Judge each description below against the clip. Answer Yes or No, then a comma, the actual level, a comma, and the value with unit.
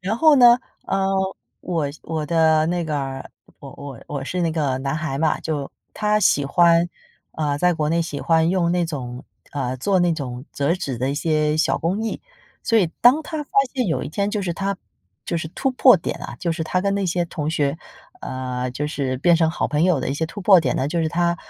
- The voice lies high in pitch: No, medium, 160 Hz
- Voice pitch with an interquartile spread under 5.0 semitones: Yes, average, 4.1 semitones